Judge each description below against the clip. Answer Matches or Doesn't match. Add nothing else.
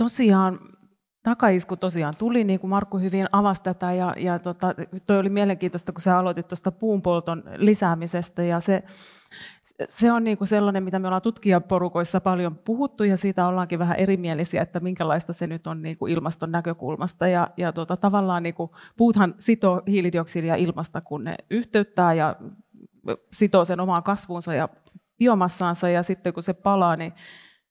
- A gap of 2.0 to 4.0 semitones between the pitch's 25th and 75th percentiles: Matches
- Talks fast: Matches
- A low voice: Doesn't match